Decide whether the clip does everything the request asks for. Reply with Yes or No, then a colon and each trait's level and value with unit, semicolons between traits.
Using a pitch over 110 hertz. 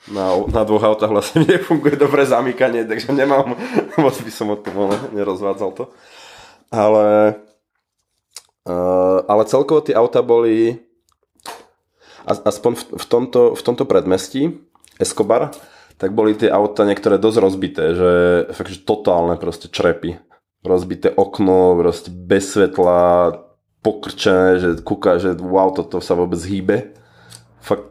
No: low, 105 Hz